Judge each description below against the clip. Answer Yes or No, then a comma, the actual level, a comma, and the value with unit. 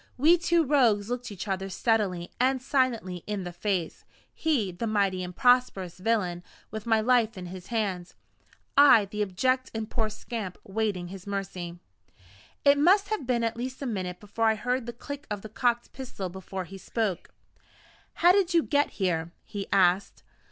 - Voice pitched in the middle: No, high, 215 Hz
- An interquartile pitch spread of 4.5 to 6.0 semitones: Yes, average, 5.0 semitones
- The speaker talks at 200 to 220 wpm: No, average, 175 wpm